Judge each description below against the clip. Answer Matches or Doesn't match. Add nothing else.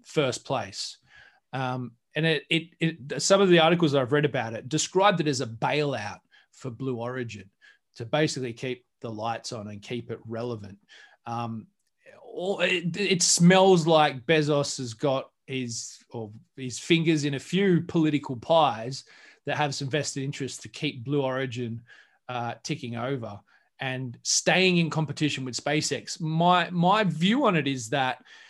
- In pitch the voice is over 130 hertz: Matches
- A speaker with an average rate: Matches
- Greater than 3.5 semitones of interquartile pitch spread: Matches